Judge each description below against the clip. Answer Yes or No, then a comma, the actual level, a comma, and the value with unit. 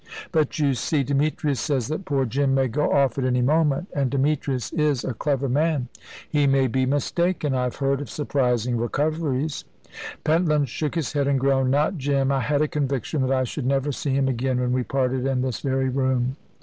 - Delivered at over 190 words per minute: Yes, average, 200 wpm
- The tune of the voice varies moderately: No, narrow, 2.3 semitones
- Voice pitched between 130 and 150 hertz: Yes, low, 135 Hz